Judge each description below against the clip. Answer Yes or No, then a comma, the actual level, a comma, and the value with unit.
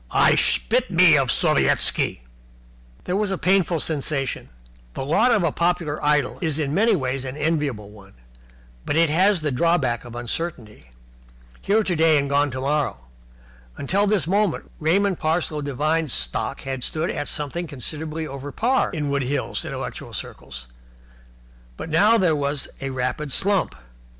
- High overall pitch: No, medium, 150 Hz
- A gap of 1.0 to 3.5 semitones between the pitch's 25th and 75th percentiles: No, average, 4.2 semitones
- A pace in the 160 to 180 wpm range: No, average, 150 wpm